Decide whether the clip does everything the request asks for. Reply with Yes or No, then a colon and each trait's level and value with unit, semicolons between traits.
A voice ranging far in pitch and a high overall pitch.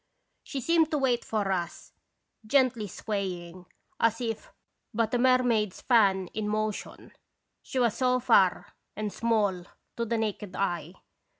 No: average, 3.8 semitones; high, 215 Hz